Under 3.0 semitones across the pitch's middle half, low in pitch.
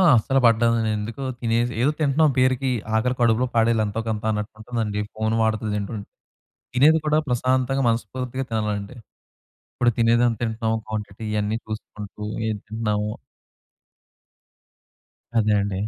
Yes: narrow, 2.6 semitones; low, 115 Hz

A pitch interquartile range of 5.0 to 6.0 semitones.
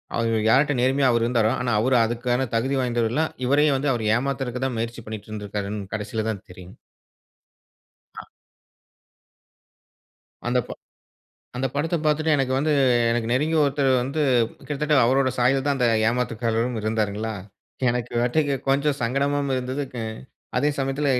No: average, 3.4 semitones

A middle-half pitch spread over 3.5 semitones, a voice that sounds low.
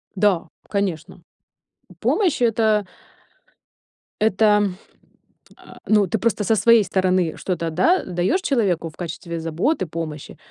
No: average, 4.6 semitones; high, 190 Hz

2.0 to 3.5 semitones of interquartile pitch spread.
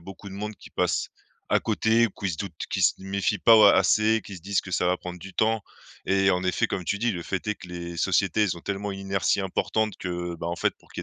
Yes: narrow, 2.6 semitones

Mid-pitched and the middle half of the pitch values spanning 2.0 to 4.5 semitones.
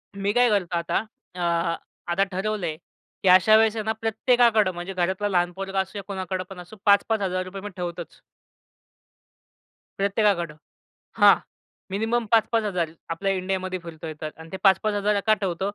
No: high, 195 Hz; average, 2.8 semitones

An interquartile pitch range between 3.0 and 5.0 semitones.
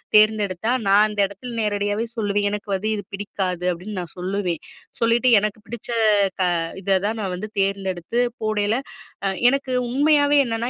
No: narrow, 2.5 semitones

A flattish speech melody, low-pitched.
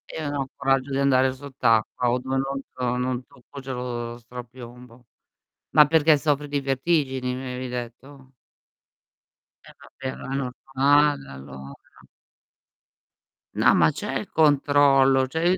Yes: narrow, 2.2 semitones; low, 130 Hz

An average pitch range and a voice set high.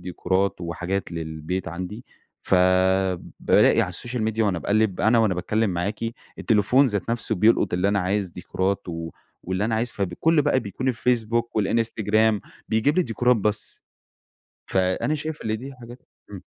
No: average, 3.9 semitones; low, 105 Hz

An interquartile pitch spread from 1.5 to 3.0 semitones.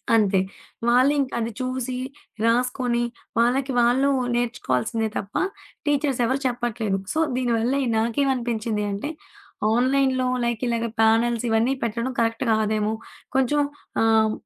Yes: narrow, 2.6 semitones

